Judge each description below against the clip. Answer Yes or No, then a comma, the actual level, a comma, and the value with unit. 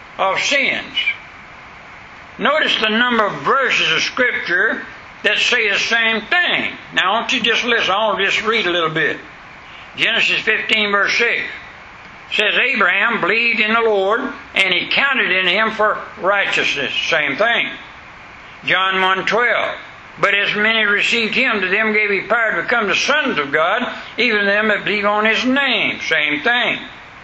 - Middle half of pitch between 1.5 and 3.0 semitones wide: Yes, narrow, 2.5 semitones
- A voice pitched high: Yes, high, 220 Hz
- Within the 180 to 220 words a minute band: No, average, 160 wpm